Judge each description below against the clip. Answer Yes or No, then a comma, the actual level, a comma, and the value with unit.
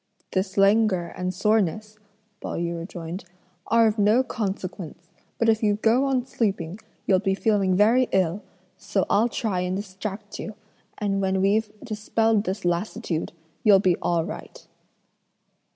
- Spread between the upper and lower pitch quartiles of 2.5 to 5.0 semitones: Yes, average, 2.9 semitones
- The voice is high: Yes, high, 200 Hz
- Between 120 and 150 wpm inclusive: Yes, average, 145 wpm